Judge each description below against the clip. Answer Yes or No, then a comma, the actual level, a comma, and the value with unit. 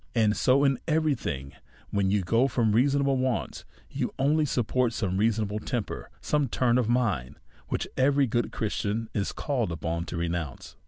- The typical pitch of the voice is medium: No, low, 115 Hz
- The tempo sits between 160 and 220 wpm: Yes, average, 170 wpm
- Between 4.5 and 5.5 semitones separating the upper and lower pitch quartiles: Yes, average, 4.8 semitones